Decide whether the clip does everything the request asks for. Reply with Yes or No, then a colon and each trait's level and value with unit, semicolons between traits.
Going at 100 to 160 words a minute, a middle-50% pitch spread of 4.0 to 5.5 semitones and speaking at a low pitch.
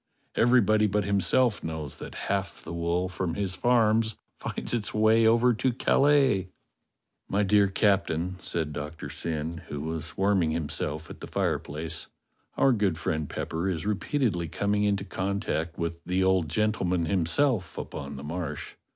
Yes: average, 150 wpm; average, 4.5 semitones; very low, 95 Hz